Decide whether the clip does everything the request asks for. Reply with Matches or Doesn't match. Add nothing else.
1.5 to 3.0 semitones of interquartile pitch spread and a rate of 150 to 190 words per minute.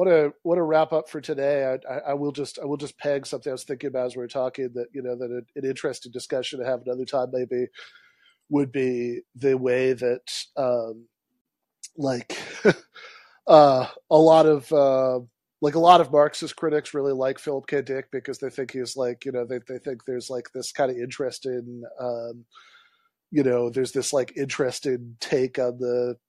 Doesn't match